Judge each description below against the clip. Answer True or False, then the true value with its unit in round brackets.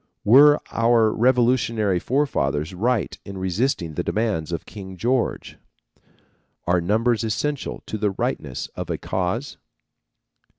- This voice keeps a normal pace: False (120 wpm)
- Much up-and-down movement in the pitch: False (4.7 semitones)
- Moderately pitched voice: False (110 Hz)